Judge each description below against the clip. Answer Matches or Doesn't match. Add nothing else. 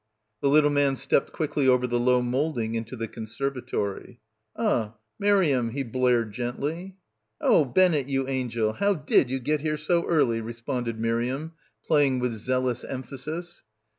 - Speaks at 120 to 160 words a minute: Matches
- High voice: Doesn't match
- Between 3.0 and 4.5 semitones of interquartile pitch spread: Matches